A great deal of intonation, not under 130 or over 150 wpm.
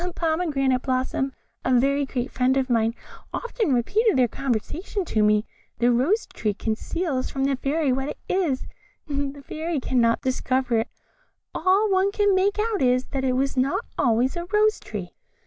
No: wide, 5.7 semitones; average, 170 wpm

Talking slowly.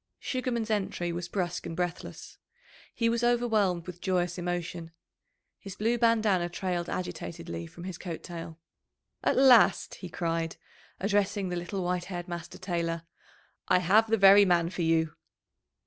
No: average, 150 wpm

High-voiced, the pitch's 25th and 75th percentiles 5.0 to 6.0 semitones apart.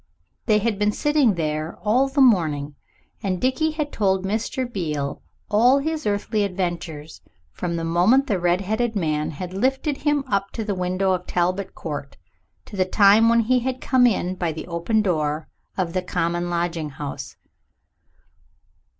Yes: high, 195 Hz; average, 5.3 semitones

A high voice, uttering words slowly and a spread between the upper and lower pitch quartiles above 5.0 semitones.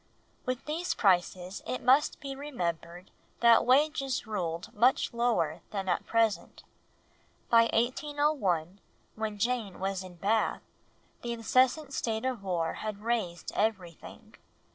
Yes: high, 220 Hz; slow, 120 wpm; wide, 5.5 semitones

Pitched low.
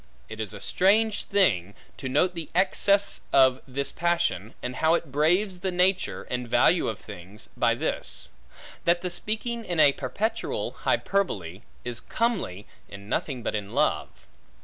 No: medium, 150 Hz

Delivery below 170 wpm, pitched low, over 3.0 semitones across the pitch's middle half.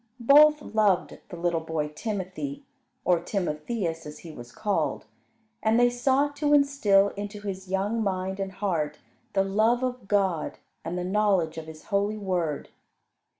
No: average, 150 wpm; high, 195 Hz; average, 4.2 semitones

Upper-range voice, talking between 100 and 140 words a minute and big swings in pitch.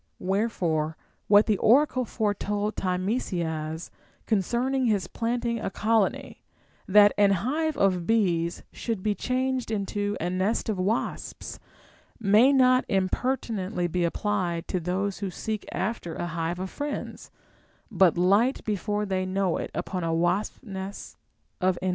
No: high, 200 Hz; slow, 135 wpm; average, 3.8 semitones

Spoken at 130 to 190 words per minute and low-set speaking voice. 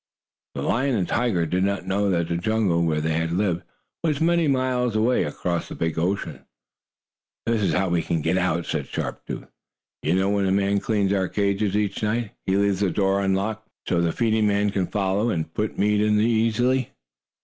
No: average, 200 wpm; low, 100 Hz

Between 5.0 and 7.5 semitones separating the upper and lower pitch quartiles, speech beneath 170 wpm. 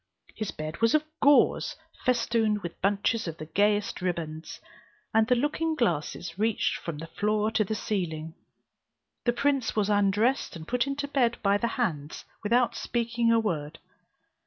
Yes: wide, 5.4 semitones; average, 160 wpm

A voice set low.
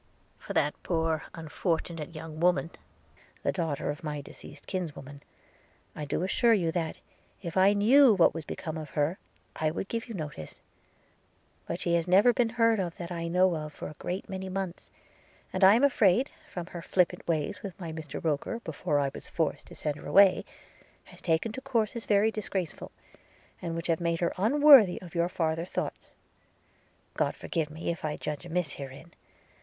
No: medium, 170 Hz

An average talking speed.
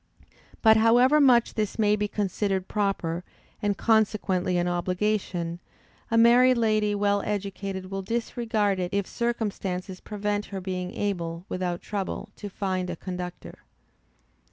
No: slow, 130 wpm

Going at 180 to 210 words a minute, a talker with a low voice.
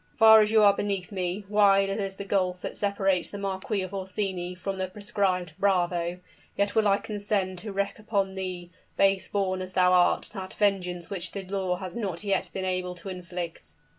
No: average, 195 wpm; high, 190 Hz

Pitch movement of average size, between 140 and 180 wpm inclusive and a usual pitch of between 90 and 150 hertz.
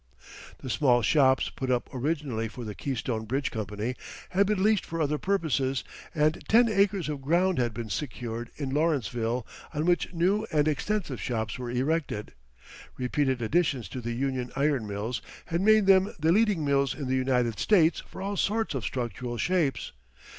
No: wide, 5.7 semitones; average, 170 wpm; medium, 140 Hz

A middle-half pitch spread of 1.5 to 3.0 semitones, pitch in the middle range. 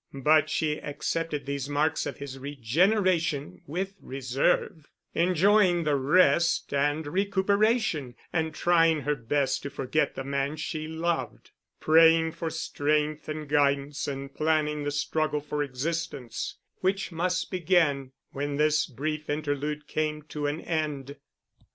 Yes: narrow, 2.6 semitones; medium, 150 Hz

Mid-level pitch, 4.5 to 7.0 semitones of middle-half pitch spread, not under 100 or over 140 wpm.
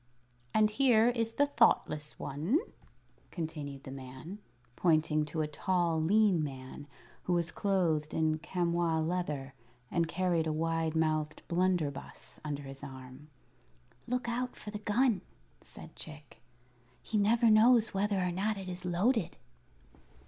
Yes: medium, 170 Hz; average, 5.3 semitones; slow, 135 wpm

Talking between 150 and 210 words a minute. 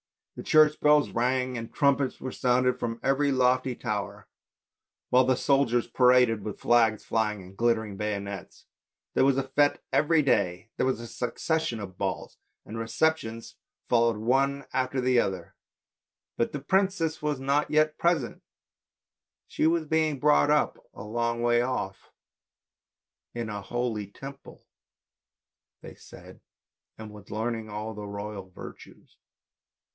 No: average, 140 wpm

